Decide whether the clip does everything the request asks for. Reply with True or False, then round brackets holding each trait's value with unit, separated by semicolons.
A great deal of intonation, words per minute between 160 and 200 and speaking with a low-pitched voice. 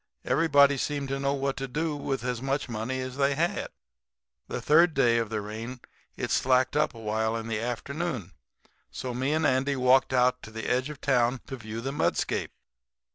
False (3.1 semitones; 190 wpm; 130 Hz)